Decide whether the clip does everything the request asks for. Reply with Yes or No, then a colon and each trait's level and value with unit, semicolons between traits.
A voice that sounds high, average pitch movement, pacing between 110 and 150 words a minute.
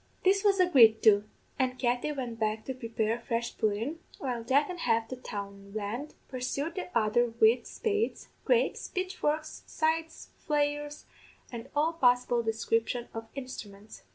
Yes: high, 245 Hz; average, 4.9 semitones; average, 145 wpm